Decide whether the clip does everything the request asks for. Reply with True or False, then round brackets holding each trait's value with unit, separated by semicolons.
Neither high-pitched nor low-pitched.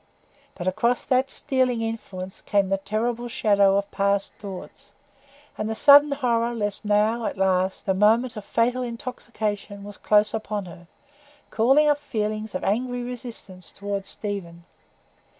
False (215 Hz)